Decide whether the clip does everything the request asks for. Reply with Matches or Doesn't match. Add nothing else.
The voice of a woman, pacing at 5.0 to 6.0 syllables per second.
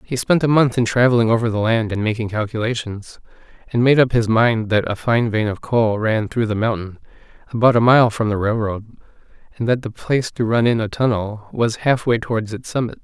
Doesn't match